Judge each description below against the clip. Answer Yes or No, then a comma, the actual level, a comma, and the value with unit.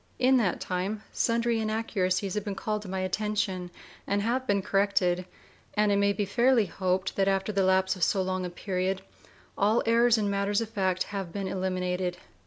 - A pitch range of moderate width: No, narrow, 2.3 semitones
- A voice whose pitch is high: Yes, high, 195 Hz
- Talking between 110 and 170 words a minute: No, average, 190 wpm